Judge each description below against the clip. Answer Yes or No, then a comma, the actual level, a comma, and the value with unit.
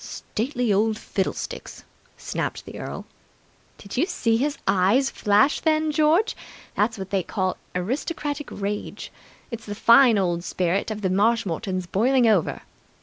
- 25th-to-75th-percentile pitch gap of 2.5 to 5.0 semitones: No, wide, 5.6 semitones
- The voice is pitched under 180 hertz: No, high, 220 Hz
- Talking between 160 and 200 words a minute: No, average, 140 wpm